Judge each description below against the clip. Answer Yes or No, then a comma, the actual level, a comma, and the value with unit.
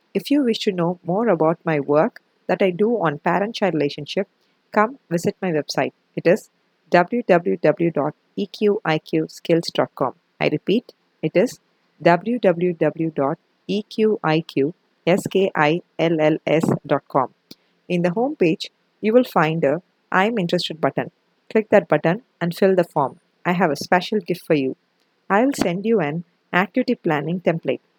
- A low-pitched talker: No, medium, 180 Hz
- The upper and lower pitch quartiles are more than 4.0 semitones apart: Yes, average, 4.6 semitones